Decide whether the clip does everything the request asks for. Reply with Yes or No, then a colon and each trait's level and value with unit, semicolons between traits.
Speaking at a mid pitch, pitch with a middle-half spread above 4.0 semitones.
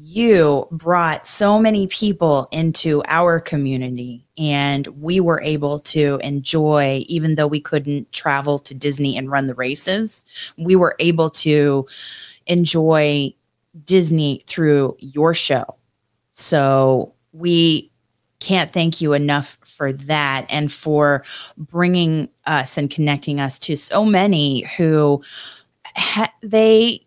No: medium, 150 Hz; average, 3.3 semitones